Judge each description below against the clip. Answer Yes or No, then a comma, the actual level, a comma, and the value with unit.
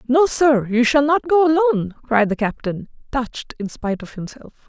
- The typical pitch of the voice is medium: No, very high, 260 Hz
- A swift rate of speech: No, average, 190 wpm